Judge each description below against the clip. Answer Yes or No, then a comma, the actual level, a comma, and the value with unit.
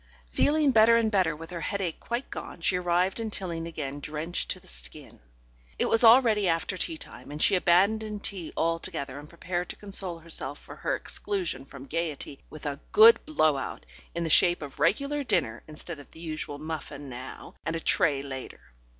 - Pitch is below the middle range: No, medium, 170 Hz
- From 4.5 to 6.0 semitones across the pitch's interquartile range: Yes, average, 5.1 semitones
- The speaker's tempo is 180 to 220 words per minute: Yes, average, 185 wpm